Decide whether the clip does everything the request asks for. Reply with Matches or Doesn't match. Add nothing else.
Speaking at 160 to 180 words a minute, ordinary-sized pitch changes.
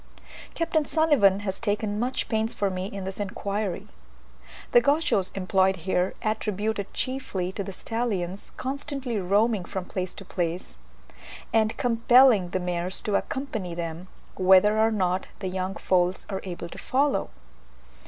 Doesn't match